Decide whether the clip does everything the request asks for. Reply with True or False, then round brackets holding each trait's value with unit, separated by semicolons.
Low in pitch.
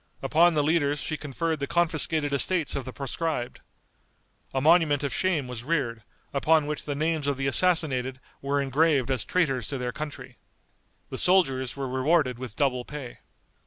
False (145 Hz)